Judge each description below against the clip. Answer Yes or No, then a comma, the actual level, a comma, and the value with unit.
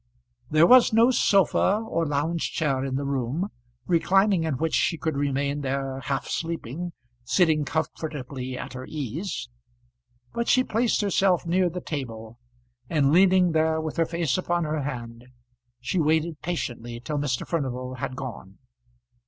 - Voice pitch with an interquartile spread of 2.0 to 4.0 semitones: No, average, 4.6 semitones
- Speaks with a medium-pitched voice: Yes, medium, 155 Hz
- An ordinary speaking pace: Yes, average, 150 wpm